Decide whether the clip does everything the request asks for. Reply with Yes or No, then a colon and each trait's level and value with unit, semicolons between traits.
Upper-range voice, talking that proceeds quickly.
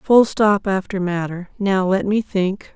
No: high, 195 Hz; average, 175 wpm